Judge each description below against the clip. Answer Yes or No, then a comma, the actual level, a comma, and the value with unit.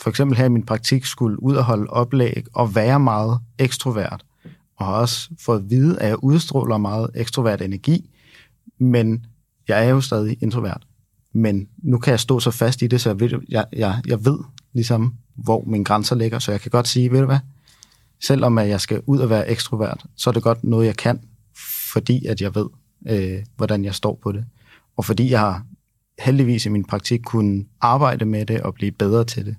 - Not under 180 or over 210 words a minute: Yes, average, 205 wpm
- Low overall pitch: Yes, low, 115 Hz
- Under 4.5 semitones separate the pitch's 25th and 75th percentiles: Yes, average, 2.9 semitones